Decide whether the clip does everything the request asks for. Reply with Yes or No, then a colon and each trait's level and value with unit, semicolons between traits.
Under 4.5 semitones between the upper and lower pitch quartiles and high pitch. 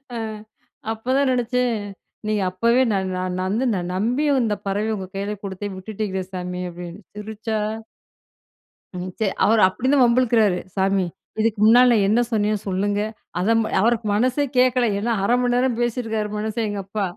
Yes: average, 3.5 semitones; high, 215 Hz